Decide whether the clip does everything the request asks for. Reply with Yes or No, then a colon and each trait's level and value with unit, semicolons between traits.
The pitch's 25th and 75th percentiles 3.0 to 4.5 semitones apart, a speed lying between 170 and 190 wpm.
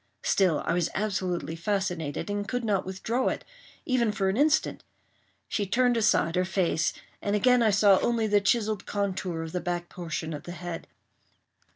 Yes: average, 3.6 semitones; average, 175 wpm